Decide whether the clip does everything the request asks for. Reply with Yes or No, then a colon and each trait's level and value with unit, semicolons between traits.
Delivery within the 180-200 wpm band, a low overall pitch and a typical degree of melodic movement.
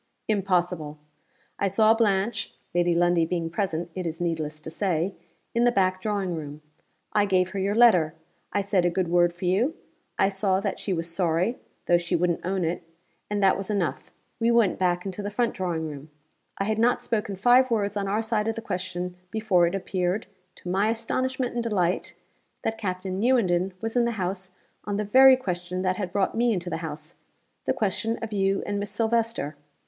No: average, 195 wpm; high, 190 Hz; average, 3.5 semitones